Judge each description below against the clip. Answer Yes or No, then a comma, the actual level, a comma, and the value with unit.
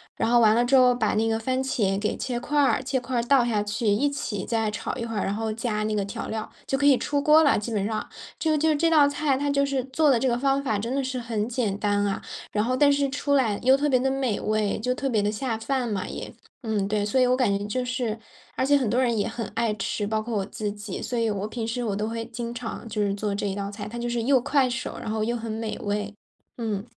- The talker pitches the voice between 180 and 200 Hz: No, high, 230 Hz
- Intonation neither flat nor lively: Yes, average, 3.7 semitones